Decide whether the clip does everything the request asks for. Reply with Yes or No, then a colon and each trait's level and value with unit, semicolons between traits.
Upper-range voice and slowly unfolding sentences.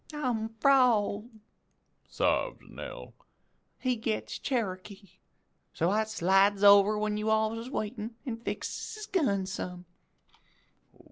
Yes: high, 220 Hz; slow, 115 wpm